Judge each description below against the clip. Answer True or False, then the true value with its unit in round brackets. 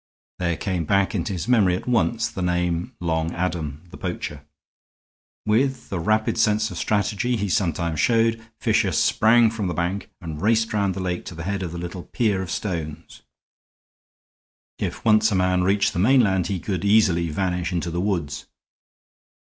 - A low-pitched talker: True (95 Hz)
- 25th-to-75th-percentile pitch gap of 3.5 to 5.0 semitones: True (3.9 semitones)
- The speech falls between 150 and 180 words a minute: True (170 wpm)